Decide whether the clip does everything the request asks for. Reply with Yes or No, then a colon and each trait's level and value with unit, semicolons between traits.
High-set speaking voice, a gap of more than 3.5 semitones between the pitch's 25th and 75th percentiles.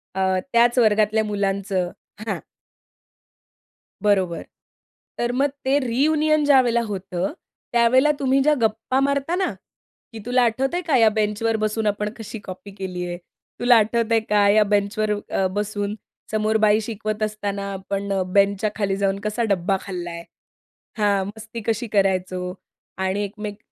No: high, 210 Hz; average, 2.8 semitones